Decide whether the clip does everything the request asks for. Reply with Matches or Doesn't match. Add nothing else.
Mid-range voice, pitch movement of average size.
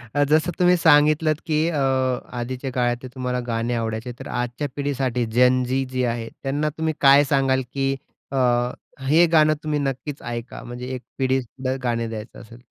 Doesn't match